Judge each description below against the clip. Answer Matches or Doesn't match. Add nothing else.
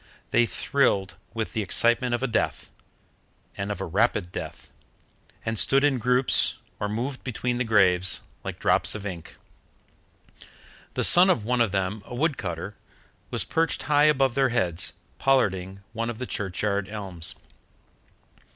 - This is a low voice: Matches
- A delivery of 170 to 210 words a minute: Doesn't match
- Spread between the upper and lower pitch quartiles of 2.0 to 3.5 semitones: Doesn't match